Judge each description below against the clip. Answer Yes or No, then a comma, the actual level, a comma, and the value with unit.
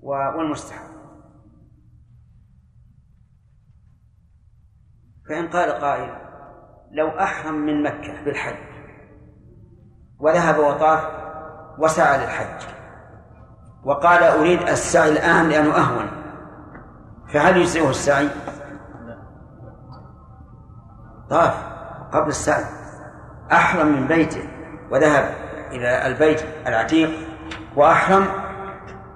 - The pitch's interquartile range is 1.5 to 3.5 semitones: No, wide, 5.5 semitones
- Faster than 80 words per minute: No, average, 70 wpm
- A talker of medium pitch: Yes, medium, 145 Hz